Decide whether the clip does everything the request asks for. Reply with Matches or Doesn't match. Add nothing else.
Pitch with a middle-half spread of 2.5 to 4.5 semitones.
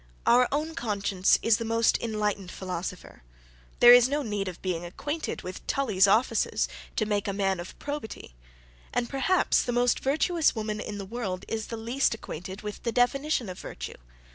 Matches